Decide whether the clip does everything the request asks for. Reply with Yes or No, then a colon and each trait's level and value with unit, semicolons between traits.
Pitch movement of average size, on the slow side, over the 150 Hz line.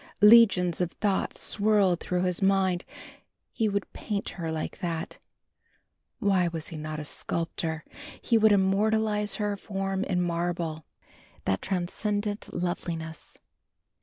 Yes: average, 3.3 semitones; slow, 125 wpm; medium, 185 Hz